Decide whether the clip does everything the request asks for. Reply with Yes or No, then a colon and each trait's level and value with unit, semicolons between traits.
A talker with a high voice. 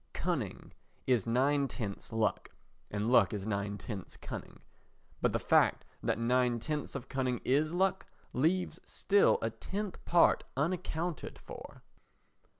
No: low, 130 Hz